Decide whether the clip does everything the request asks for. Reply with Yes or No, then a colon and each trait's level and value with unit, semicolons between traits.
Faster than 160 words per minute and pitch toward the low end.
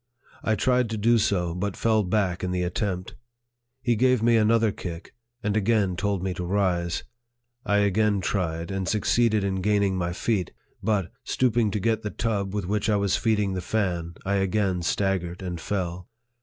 Yes: average, 180 wpm; low, 100 Hz